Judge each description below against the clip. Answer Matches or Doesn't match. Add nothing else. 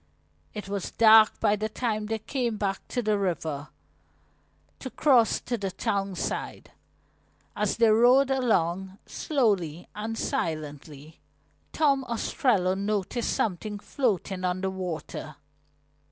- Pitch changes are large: Doesn't match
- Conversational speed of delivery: Doesn't match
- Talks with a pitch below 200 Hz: Doesn't match